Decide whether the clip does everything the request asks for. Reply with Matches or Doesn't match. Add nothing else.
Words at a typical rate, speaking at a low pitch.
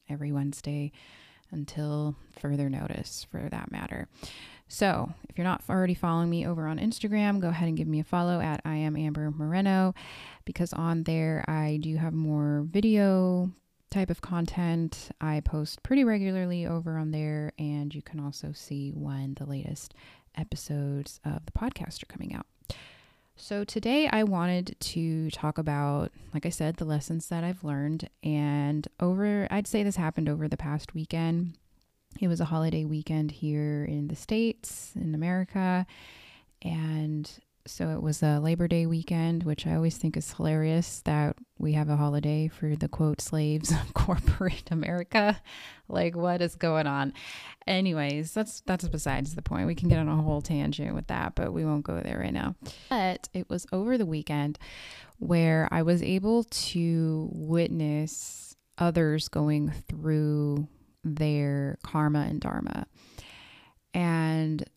Doesn't match